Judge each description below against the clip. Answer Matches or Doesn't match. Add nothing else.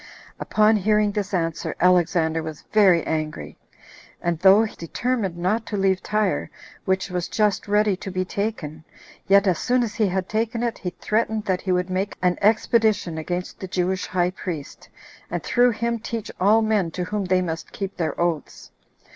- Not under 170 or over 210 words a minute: Matches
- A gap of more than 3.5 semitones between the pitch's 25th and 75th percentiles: Doesn't match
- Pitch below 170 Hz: Doesn't match